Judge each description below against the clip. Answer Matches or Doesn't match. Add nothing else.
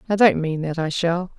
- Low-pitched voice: Doesn't match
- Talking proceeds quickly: Matches